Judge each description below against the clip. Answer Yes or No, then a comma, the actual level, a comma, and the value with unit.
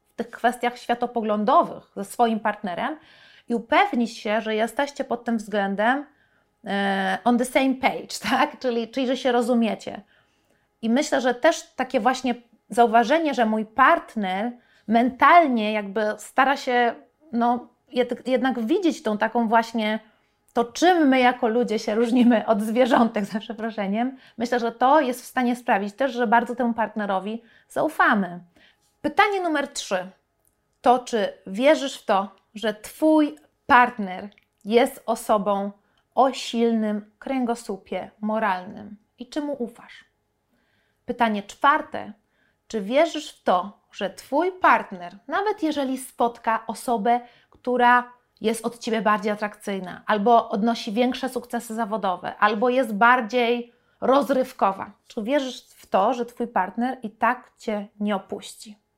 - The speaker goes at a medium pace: Yes, average, 130 wpm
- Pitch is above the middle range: Yes, high, 235 Hz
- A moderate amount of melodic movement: Yes, average, 3.1 semitones